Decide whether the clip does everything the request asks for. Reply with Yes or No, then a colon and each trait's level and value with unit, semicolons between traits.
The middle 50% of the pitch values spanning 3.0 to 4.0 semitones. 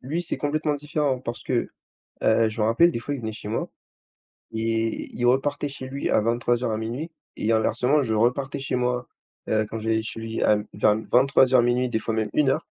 Yes: average, 3.5 semitones